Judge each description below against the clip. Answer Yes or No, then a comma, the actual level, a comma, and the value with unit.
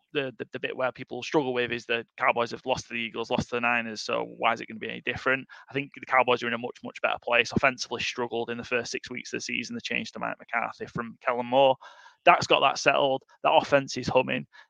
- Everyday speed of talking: No, fast, 270 wpm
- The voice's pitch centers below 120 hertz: No, low, 125 Hz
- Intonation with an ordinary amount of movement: No, narrow, 2.1 semitones